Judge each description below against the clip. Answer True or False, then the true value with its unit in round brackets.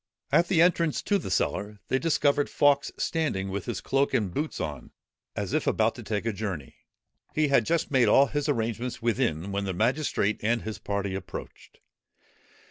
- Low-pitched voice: True (115 Hz)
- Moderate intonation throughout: False (6.4 semitones)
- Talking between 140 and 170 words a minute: False (180 wpm)